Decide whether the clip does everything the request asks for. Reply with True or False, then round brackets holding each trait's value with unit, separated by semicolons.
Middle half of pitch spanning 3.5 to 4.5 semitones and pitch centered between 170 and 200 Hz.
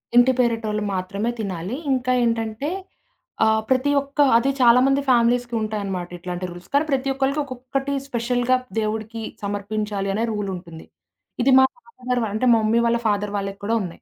False (3.8 semitones; 230 Hz)